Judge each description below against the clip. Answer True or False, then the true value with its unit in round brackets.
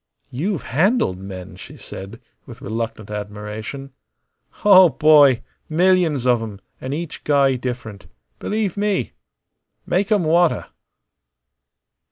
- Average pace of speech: False (110 wpm)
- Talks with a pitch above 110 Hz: True (135 Hz)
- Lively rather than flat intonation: True (8.1 semitones)